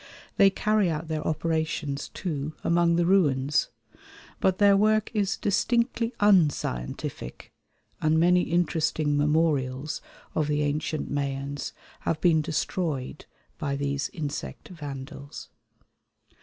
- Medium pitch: Yes, medium, 155 Hz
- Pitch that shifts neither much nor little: Yes, average, 3.7 semitones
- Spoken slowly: Yes, slow, 110 wpm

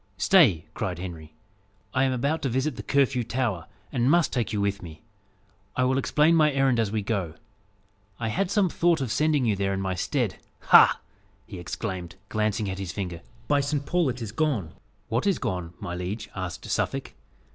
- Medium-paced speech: Yes, average, 190 wpm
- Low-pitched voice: Yes, low, 115 Hz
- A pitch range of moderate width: No, wide, 6.7 semitones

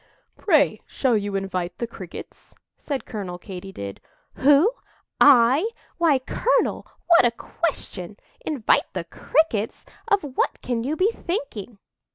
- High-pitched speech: Yes, high, 245 Hz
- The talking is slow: Yes, slow, 130 wpm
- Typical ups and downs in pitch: No, wide, 7.4 semitones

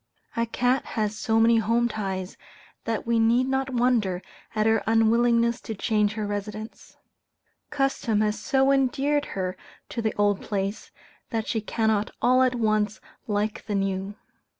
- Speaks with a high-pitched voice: Yes, high, 225 Hz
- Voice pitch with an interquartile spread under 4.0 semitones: Yes, narrow, 2.4 semitones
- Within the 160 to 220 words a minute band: No, average, 150 wpm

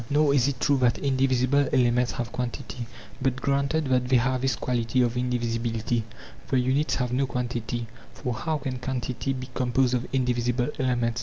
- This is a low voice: Yes, low, 125 Hz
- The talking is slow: No, average, 170 wpm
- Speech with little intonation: Yes, narrow, 1.7 semitones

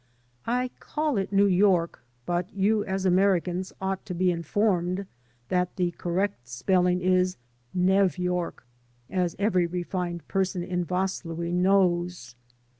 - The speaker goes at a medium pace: No, slow, 125 wpm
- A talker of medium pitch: Yes, medium, 180 Hz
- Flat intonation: Yes, narrow, 1.7 semitones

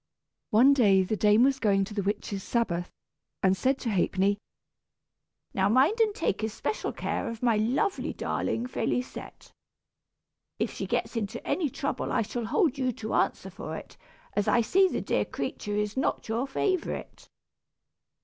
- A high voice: Yes, high, 230 Hz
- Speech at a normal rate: Yes, average, 160 wpm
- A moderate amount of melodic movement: Yes, average, 4.5 semitones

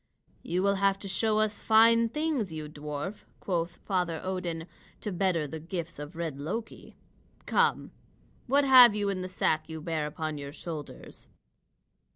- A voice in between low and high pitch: Yes, medium, 180 Hz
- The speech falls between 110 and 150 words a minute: No, average, 160 wpm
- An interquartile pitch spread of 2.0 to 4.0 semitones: No, average, 4.8 semitones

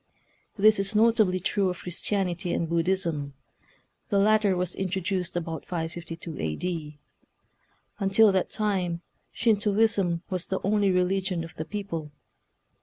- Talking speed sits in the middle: No, slow, 130 wpm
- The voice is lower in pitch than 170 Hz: No, medium, 185 Hz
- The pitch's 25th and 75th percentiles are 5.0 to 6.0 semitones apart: No, average, 3.0 semitones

